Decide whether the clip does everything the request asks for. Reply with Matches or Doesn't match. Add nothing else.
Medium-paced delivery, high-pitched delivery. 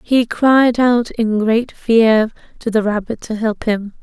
Matches